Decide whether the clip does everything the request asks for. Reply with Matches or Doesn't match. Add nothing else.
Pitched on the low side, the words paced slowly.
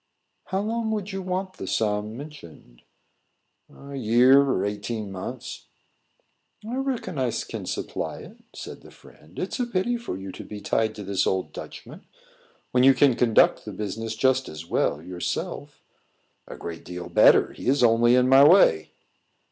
Doesn't match